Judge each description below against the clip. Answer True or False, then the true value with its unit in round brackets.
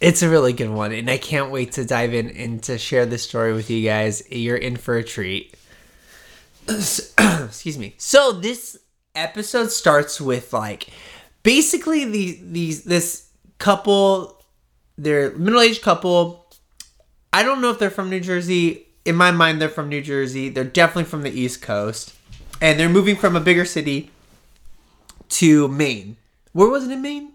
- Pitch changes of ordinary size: False (7.9 semitones)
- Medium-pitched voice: True (155 Hz)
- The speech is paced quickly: False (170 wpm)